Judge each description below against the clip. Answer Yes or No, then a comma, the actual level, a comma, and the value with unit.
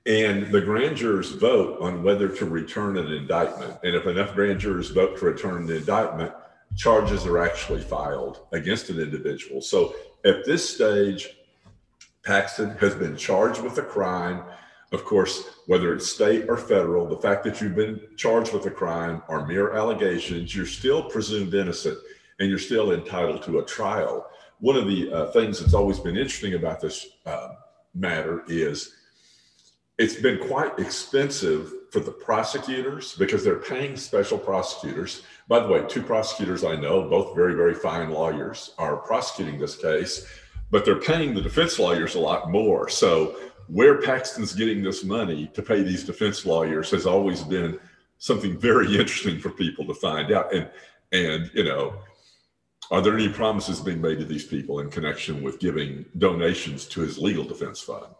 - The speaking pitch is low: Yes, low, 105 Hz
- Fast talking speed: No, average, 170 wpm